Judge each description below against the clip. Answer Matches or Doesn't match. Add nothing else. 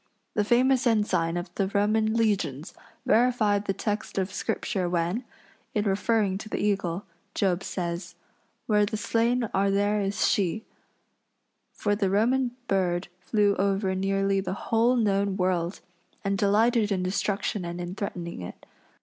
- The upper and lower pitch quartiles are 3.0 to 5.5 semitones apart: Doesn't match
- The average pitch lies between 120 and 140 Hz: Doesn't match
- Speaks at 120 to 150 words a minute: Matches